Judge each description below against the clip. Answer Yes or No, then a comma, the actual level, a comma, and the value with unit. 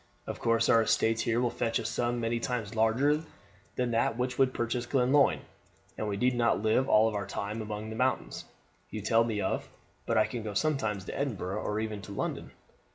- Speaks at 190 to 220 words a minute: Yes, average, 200 wpm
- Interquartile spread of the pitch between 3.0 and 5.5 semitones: No, narrow, 2.4 semitones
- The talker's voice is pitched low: Yes, low, 115 Hz